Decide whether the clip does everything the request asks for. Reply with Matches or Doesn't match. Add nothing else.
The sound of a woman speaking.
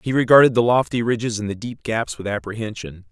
Doesn't match